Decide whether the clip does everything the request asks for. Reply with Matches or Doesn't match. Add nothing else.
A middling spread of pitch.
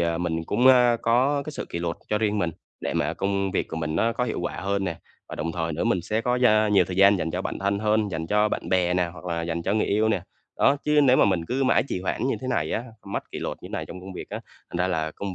Matches